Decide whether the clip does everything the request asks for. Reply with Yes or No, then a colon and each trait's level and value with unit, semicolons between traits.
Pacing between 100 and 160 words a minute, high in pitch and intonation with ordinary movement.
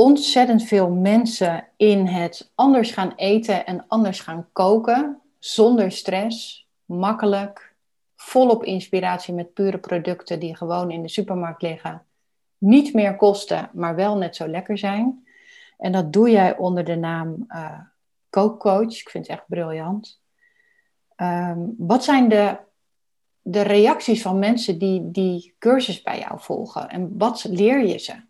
Yes: average, 145 wpm; high, 200 Hz; average, 4.0 semitones